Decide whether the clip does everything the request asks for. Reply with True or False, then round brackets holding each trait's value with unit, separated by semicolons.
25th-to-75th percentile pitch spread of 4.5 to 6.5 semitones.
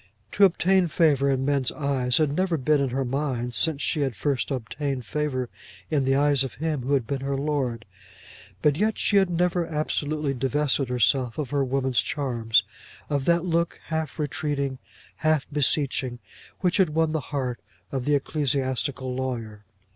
False (2.8 semitones)